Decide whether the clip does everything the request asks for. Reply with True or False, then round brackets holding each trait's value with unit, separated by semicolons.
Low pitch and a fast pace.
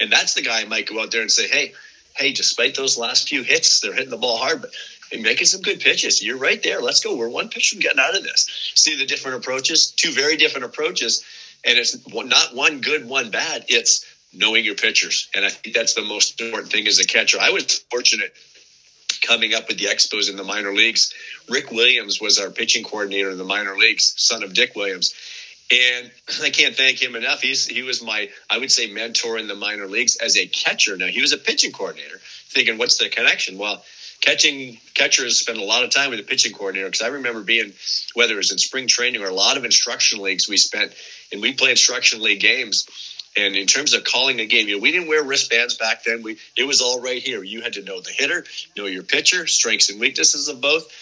True (130 Hz; 235 wpm)